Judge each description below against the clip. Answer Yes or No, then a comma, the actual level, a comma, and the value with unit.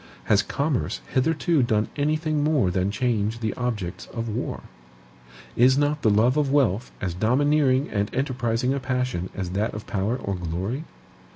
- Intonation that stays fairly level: No, average, 5.2 semitones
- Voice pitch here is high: No, low, 120 Hz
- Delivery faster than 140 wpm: Yes, average, 160 wpm